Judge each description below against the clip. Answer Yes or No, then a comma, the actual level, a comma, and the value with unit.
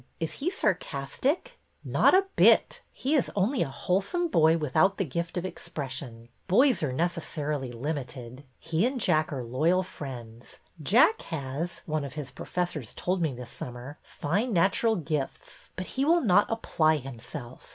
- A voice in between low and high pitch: Yes, medium, 160 Hz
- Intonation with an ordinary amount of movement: No, wide, 6.3 semitones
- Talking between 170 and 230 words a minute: No, average, 160 wpm